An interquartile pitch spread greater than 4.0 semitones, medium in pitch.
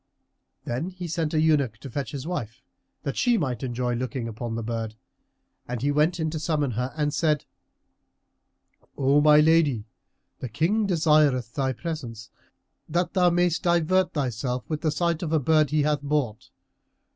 Yes: average, 4.5 semitones; medium, 150 Hz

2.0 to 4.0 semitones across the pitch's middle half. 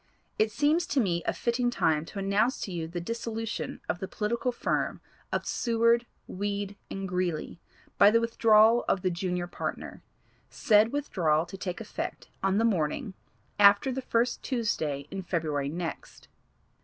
No: average, 4.8 semitones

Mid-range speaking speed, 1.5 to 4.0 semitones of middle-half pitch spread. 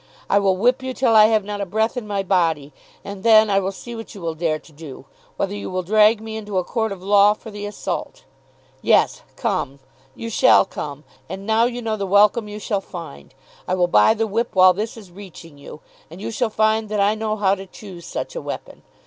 No: fast, 235 wpm; average, 3.0 semitones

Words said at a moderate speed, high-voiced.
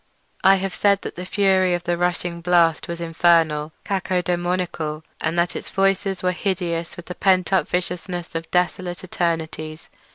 No: average, 150 wpm; medium, 175 Hz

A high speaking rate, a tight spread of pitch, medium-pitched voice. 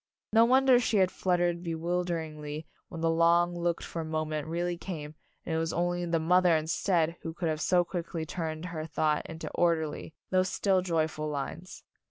No: average, 180 wpm; narrow, 1.9 semitones; medium, 170 Hz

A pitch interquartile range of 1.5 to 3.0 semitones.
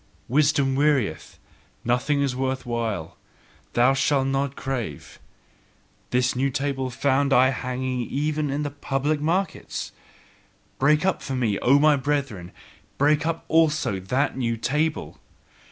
Yes: average, 2.7 semitones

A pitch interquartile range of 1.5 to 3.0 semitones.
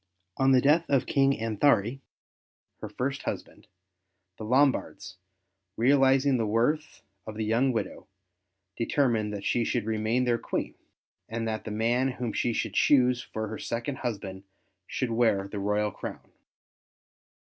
No: average, 3.5 semitones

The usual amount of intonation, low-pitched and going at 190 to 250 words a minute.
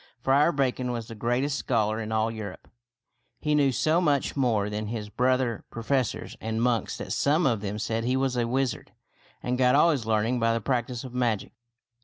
Yes: average, 3.1 semitones; low, 120 Hz; average, 195 wpm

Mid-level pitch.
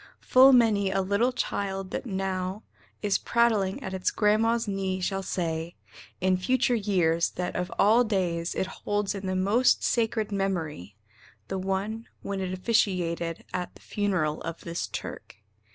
No: high, 195 Hz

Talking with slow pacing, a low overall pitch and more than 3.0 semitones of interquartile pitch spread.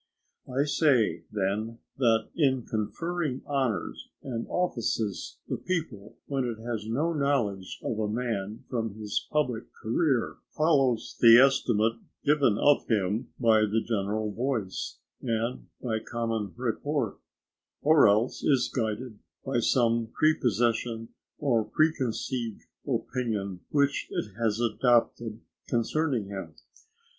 Yes: slow, 115 wpm; low, 115 Hz; average, 3.7 semitones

